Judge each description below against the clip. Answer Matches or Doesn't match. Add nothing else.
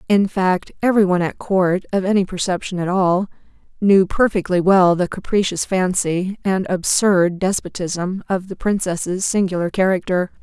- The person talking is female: Matches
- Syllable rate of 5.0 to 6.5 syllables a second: Doesn't match